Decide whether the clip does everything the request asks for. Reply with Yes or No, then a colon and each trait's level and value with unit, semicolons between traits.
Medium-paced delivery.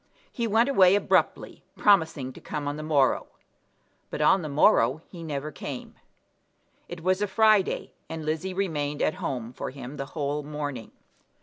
Yes: average, 165 wpm